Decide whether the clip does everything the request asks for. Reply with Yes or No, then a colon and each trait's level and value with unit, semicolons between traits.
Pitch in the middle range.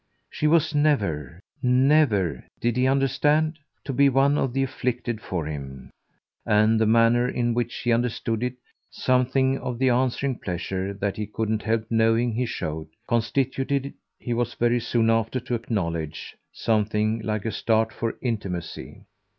No: low, 115 Hz